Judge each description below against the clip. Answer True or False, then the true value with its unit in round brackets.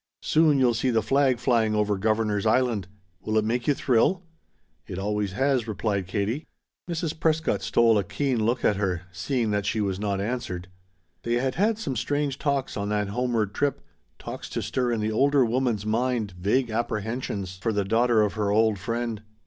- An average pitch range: True (3.8 semitones)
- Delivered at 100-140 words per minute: False (185 wpm)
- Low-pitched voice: True (115 Hz)